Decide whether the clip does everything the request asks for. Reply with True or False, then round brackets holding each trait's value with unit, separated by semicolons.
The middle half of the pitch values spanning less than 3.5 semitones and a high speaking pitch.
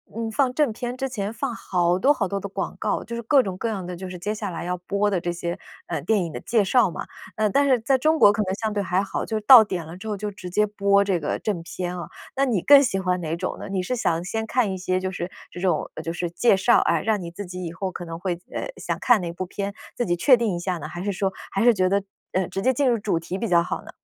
False (3.8 semitones; 195 Hz)